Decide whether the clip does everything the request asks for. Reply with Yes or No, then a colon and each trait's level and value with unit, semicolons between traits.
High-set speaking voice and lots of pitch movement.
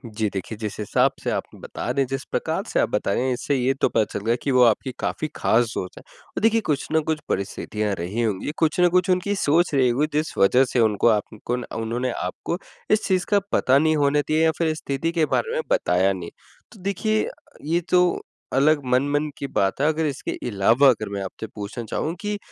No: low, 135 Hz; wide, 6.2 semitones